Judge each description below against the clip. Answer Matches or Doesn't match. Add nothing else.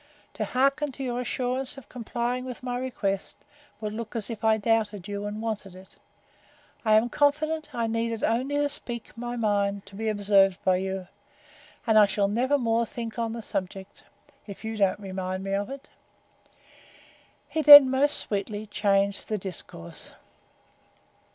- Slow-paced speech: Doesn't match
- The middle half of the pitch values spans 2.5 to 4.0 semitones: Matches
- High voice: Matches